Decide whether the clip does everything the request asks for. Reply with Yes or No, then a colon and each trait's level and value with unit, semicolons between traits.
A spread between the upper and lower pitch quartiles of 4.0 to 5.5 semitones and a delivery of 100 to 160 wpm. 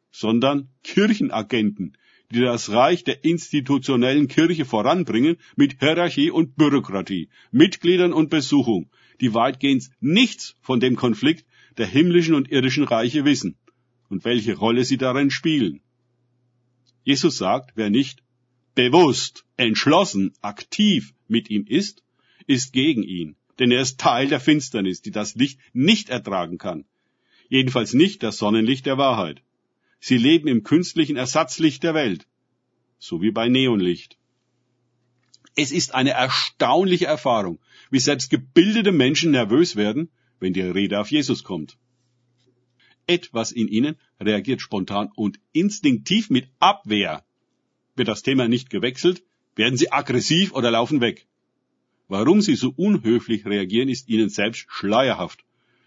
Yes: average, 4.8 semitones; average, 130 wpm